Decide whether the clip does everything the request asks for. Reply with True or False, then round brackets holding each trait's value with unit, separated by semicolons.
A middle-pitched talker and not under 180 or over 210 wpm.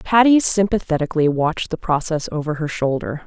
False (165 Hz; 145 wpm)